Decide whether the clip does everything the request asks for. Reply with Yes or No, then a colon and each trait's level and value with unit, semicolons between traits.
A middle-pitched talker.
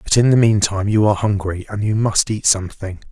No: low, 105 Hz